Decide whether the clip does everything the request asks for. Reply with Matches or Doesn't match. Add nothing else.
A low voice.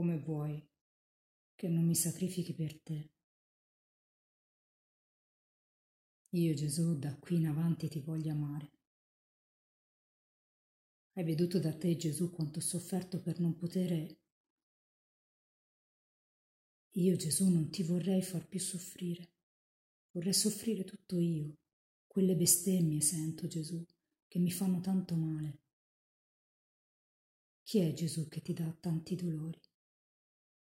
Doesn't match